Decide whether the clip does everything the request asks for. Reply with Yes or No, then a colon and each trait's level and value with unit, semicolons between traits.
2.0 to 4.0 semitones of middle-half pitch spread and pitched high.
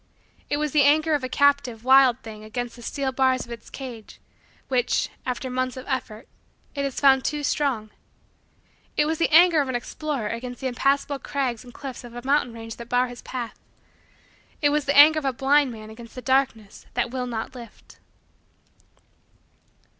Yes: average, 2.9 semitones; very high, 260 Hz